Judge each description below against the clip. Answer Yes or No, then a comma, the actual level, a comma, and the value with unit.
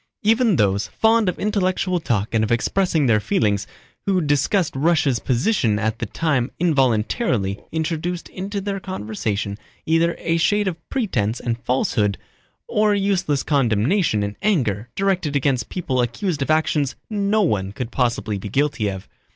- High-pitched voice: No, medium, 145 Hz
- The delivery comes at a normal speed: Yes, average, 150 wpm